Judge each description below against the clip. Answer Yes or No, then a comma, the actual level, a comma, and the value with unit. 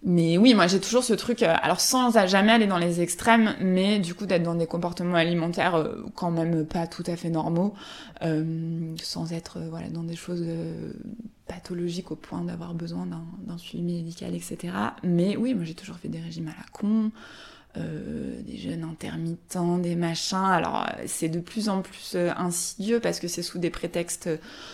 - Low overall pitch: No, medium, 175 Hz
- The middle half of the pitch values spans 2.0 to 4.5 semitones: Yes, average, 3.3 semitones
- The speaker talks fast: No, average, 185 wpm